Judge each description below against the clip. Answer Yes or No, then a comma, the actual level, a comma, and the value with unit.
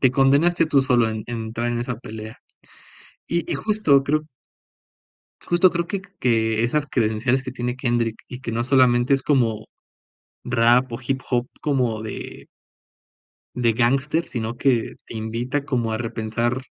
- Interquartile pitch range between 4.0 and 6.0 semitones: No, average, 2.9 semitones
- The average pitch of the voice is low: Yes, low, 125 Hz